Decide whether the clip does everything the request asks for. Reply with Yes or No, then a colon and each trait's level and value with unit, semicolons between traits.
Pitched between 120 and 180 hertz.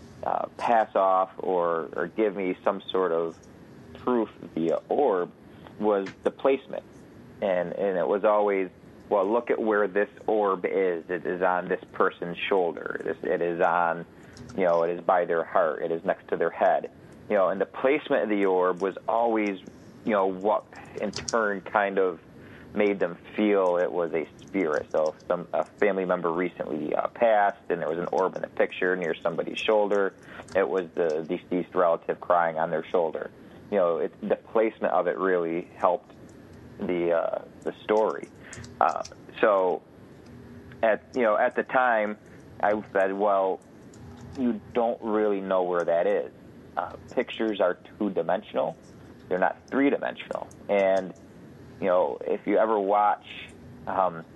No: very low, 95 Hz